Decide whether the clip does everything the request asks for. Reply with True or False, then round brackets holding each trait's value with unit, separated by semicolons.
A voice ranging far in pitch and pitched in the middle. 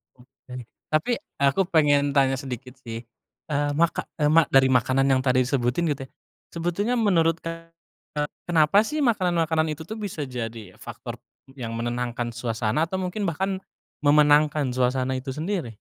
False (4.7 semitones; 145 Hz)